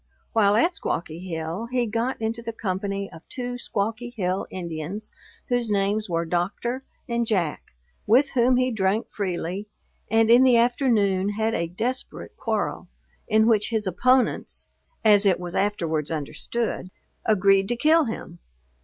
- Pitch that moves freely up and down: No, average, 4.2 semitones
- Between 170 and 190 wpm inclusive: No, average, 145 wpm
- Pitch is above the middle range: Yes, high, 215 Hz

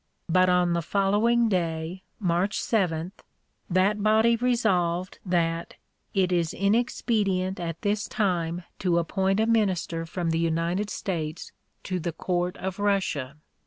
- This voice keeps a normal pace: No, slow, 130 wpm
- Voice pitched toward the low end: No, medium, 185 Hz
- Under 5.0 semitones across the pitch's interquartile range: Yes, average, 3.3 semitones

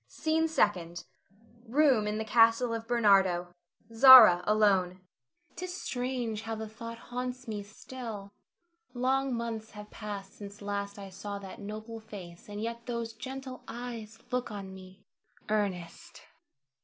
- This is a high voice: Yes, high, 220 Hz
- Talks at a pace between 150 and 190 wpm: No, average, 140 wpm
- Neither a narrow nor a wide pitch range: Yes, average, 3.3 semitones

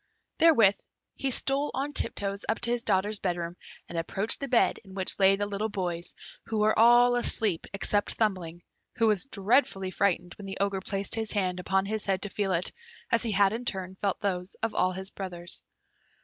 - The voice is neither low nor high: No, high, 200 Hz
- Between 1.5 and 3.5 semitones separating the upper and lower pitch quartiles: Yes, average, 2.9 semitones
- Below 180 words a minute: No, average, 200 wpm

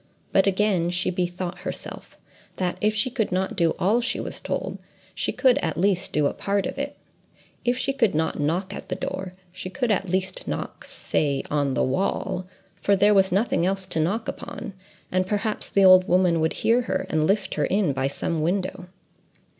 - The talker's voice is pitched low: No, medium, 185 Hz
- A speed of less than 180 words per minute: No, average, 185 wpm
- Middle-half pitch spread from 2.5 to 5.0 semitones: Yes, average, 2.8 semitones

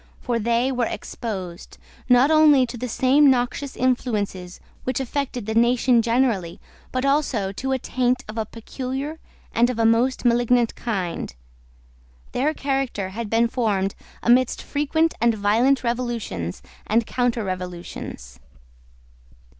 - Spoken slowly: Yes, slow, 130 wpm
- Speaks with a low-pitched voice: No, high, 240 Hz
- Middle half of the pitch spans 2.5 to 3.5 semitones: Yes, average, 3.1 semitones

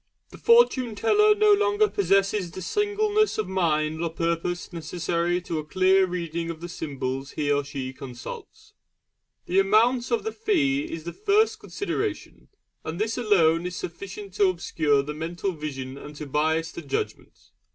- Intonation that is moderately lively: No, wide, 6.5 semitones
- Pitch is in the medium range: Yes, medium, 175 Hz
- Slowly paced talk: No, average, 160 wpm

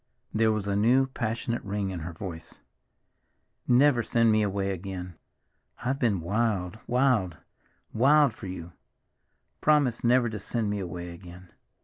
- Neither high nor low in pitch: No, low, 105 Hz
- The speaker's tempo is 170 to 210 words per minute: No, average, 140 wpm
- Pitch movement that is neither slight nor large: Yes, average, 4.5 semitones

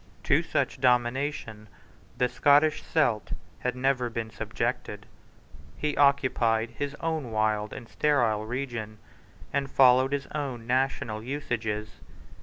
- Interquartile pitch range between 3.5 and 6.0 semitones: Yes, average, 3.8 semitones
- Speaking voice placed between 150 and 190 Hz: No, low, 125 Hz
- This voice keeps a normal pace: No, slow, 115 wpm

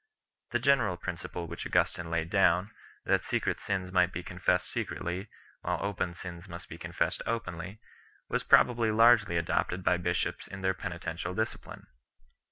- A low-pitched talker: Yes, very low, 90 Hz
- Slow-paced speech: No, average, 155 wpm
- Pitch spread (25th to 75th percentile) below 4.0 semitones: Yes, average, 2.7 semitones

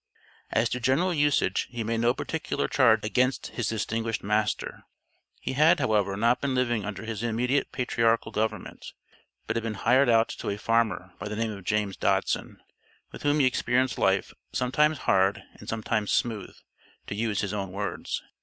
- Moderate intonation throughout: Yes, average, 3.1 semitones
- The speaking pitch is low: Yes, low, 115 Hz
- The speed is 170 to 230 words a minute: Yes, average, 175 wpm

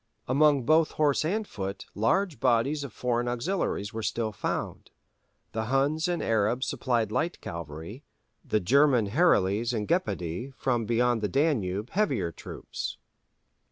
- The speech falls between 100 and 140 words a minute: Yes, slow, 135 wpm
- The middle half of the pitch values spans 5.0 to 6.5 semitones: Yes, wide, 5.5 semitones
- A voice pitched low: Yes, low, 120 Hz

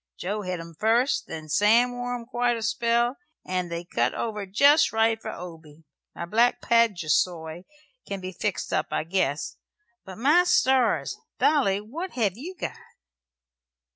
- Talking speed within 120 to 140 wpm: No, average, 155 wpm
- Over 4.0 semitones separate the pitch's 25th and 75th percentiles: Yes, average, 5.3 semitones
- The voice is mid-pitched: No, high, 215 Hz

